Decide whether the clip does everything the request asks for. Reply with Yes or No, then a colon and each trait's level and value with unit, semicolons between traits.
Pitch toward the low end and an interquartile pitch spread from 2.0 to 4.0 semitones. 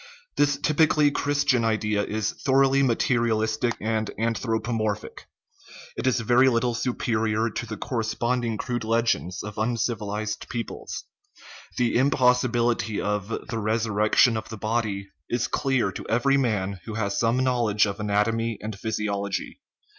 Yes: low, 115 Hz; narrow, 2.4 semitones